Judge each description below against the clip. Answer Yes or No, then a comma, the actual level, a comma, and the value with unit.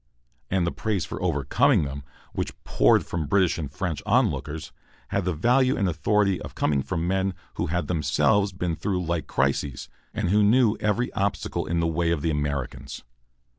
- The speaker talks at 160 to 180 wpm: Yes, average, 175 wpm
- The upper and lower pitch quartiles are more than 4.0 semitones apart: Yes, average, 4.8 semitones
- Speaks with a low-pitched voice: Yes, very low, 85 Hz